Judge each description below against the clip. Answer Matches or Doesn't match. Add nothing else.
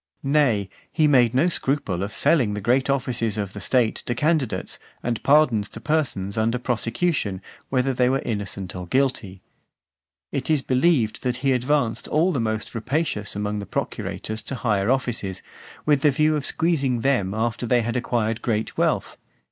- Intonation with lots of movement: Doesn't match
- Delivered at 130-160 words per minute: Doesn't match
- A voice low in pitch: Matches